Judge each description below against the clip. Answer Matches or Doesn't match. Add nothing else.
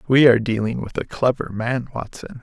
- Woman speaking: Doesn't match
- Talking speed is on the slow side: Doesn't match